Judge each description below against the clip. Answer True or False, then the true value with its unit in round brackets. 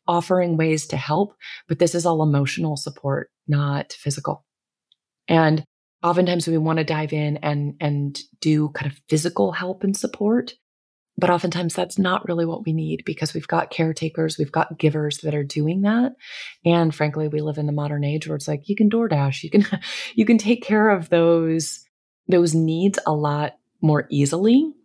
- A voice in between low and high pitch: True (160 Hz)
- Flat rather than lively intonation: False (3.2 semitones)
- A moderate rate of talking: True (180 wpm)